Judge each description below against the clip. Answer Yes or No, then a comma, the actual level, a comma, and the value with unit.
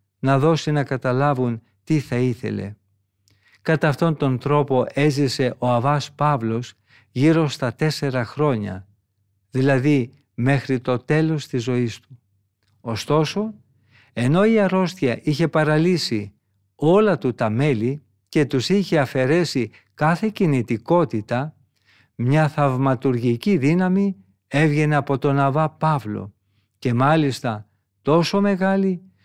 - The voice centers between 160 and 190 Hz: No, low, 135 Hz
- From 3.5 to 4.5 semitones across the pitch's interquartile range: No, average, 5.2 semitones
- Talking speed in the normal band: No, slow, 110 wpm